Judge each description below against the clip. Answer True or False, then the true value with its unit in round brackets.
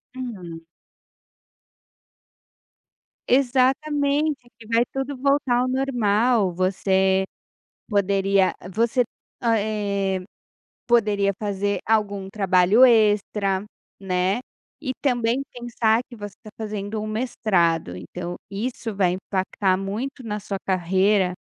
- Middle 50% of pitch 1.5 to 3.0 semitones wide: False (4.0 semitones)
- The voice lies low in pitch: False (210 Hz)